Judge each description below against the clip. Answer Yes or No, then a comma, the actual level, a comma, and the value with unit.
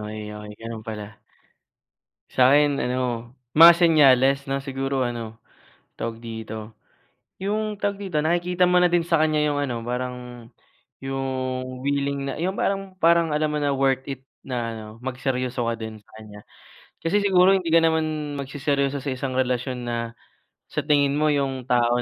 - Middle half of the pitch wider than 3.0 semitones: Yes, average, 4.0 semitones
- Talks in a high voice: No, low, 135 Hz